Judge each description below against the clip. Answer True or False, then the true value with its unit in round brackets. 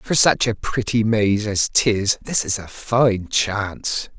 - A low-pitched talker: True (110 Hz)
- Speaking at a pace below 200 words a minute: True (170 wpm)